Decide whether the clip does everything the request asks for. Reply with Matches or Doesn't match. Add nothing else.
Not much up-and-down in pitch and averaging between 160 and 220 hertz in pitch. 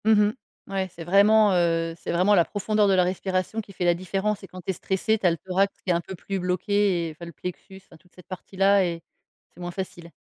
Matches